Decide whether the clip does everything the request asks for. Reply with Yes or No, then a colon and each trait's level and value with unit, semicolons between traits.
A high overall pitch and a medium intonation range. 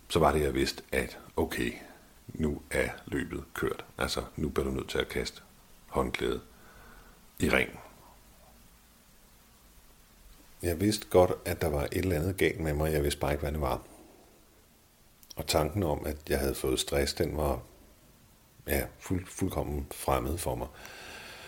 No: very low, 75 Hz; average, 3.5 semitones